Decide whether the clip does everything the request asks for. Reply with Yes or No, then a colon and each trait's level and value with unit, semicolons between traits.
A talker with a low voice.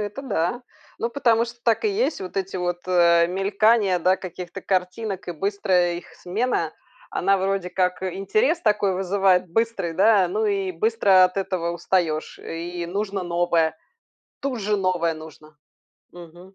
No: medium, 185 Hz